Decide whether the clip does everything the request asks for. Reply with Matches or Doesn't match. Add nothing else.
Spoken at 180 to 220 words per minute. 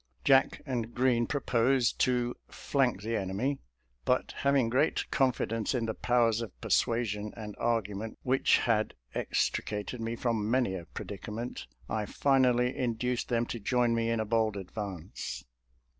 Doesn't match